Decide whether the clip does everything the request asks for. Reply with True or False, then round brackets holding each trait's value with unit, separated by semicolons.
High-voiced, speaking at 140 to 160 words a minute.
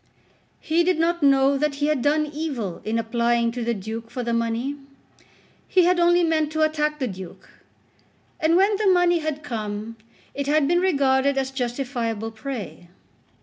False (275 Hz; 170 wpm)